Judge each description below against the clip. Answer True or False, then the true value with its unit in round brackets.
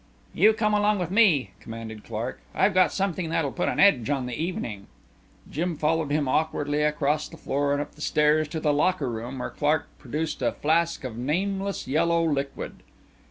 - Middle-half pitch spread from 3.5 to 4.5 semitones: True (3.9 semitones)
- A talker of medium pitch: True (150 Hz)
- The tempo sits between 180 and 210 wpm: True (185 wpm)